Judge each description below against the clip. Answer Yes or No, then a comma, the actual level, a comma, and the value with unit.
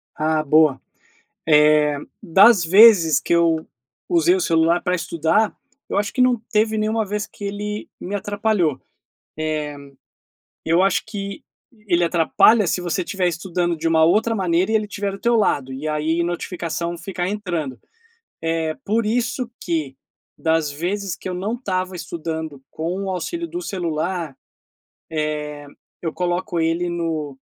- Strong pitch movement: No, average, 4.1 semitones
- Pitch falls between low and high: Yes, medium, 175 Hz